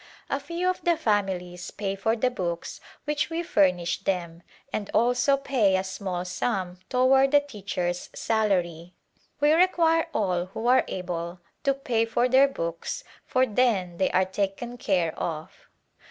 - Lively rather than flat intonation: Yes, wide, 6.4 semitones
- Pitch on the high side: Yes, high, 205 Hz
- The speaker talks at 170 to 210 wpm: No, average, 155 wpm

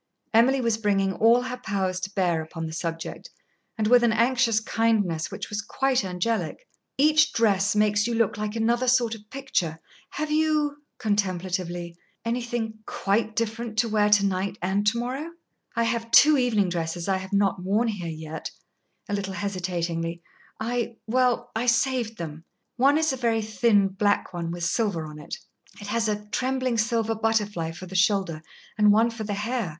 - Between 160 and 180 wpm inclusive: Yes, average, 175 wpm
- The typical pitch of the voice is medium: No, high, 215 Hz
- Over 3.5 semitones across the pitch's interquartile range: Yes, average, 3.9 semitones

